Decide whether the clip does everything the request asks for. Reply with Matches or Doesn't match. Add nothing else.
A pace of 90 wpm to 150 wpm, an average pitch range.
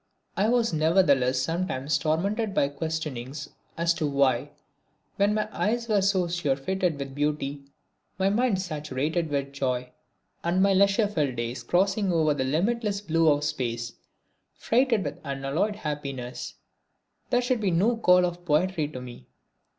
Doesn't match